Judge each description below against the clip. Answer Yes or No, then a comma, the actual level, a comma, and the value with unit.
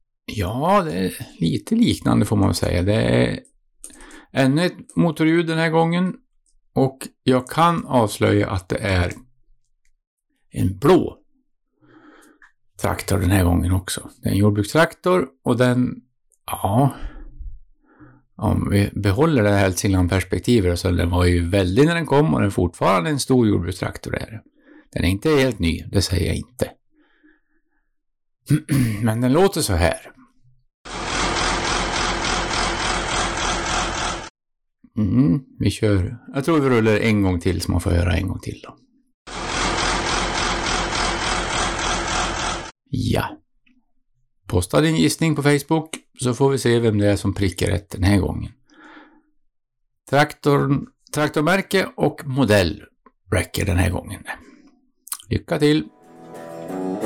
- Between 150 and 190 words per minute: No, average, 130 wpm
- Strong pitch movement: Yes, wide, 7.7 semitones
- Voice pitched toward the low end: Yes, low, 120 Hz